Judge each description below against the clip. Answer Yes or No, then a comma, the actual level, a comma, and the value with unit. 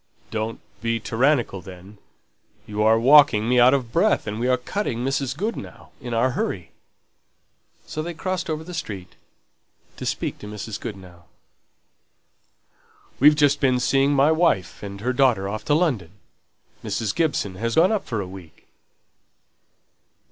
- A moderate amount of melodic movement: No, wide, 5.7 semitones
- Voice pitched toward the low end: Yes, low, 120 Hz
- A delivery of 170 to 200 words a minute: No, average, 145 wpm